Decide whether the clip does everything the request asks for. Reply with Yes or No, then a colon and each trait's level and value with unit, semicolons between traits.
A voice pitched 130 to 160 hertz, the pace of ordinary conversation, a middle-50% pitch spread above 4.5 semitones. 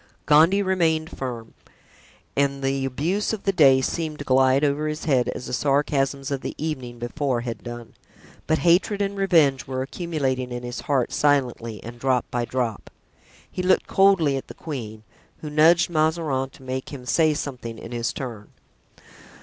No: medium, 140 Hz; average, 170 wpm; average, 4.0 semitones